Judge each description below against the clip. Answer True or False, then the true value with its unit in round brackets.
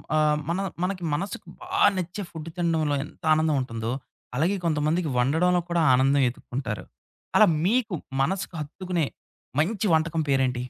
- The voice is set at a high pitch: False (160 Hz)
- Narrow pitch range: False (4.2 semitones)